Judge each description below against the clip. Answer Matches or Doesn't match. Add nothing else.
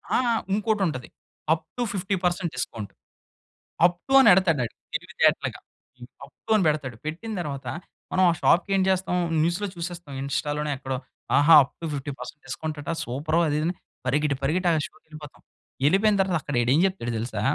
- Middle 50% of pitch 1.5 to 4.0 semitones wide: Doesn't match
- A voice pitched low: Doesn't match